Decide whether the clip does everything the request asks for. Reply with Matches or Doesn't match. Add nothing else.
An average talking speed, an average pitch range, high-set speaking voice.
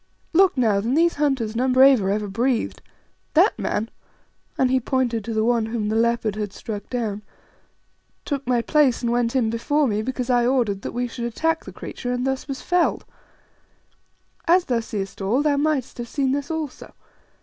Matches